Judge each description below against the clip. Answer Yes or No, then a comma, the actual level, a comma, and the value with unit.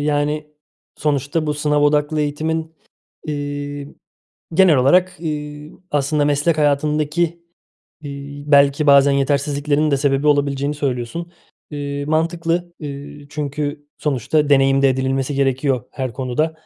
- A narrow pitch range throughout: Yes, narrow, 1.4 semitones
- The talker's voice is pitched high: No, medium, 145 Hz